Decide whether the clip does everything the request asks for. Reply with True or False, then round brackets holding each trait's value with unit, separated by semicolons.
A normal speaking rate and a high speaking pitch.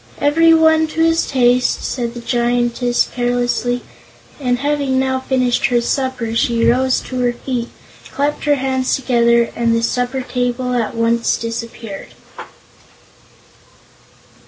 False (130 wpm; 245 Hz)